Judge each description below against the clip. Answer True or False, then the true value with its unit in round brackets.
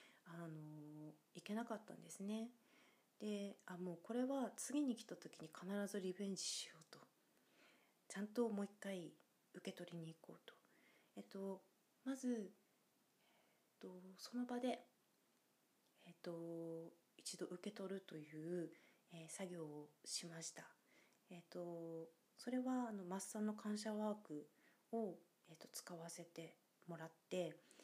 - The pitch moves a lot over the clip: False (4.2 semitones)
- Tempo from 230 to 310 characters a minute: True (250 characters per minute)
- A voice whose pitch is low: False (190 Hz)